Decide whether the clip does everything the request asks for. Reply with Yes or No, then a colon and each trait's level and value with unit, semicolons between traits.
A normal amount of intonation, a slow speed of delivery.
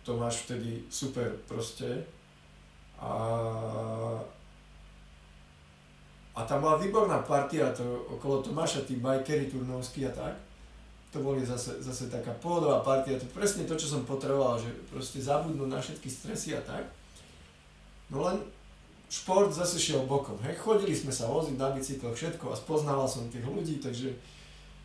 No: average, 4.6 semitones; average, 140 wpm